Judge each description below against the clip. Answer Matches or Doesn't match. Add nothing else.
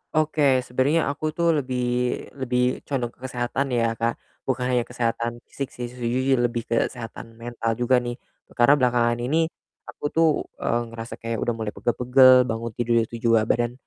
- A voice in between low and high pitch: Doesn't match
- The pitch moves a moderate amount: Doesn't match